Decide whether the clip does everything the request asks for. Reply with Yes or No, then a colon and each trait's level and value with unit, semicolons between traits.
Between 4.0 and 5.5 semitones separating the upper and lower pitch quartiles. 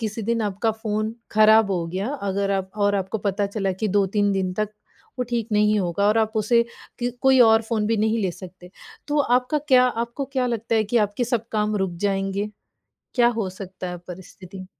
No: average, 2.8 semitones